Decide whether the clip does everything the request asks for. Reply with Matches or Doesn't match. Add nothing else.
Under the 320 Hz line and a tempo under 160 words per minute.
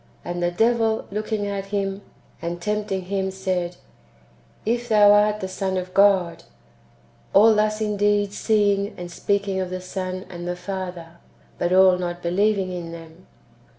Doesn't match